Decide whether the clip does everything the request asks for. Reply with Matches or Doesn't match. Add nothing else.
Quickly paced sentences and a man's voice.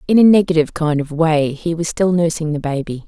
Doesn't match